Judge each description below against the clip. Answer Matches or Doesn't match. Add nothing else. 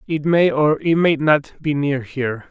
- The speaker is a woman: Doesn't match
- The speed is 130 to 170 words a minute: Doesn't match